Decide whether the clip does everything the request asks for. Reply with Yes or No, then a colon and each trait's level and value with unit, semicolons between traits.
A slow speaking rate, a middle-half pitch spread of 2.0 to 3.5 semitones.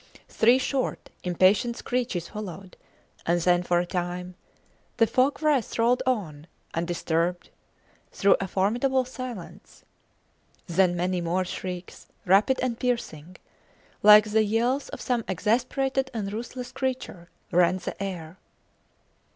No: slow, 120 wpm; wide, 5.6 semitones